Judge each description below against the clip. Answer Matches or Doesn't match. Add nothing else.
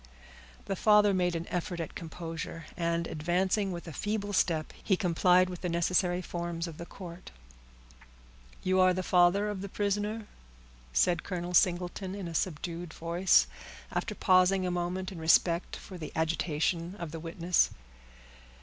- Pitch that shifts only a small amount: Matches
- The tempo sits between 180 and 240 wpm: Doesn't match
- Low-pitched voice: Doesn't match